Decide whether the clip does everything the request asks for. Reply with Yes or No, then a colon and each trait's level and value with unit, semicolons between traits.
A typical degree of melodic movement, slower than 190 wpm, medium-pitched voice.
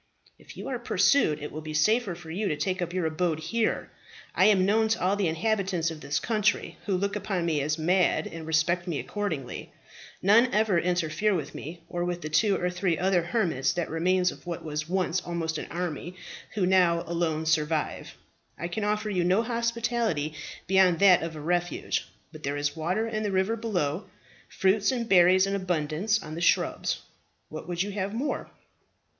No: average, 3.8 semitones; average, 195 wpm; medium, 180 Hz